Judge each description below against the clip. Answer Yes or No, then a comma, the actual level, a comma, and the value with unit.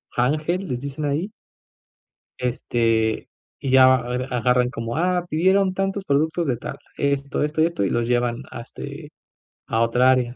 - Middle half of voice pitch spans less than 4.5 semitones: No, average, 4.8 semitones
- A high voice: No, low, 130 Hz